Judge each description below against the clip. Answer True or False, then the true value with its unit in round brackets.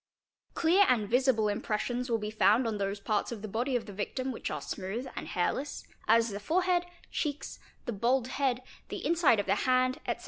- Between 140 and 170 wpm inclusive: False (200 wpm)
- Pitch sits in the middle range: False (240 Hz)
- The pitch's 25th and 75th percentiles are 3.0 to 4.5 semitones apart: True (3.8 semitones)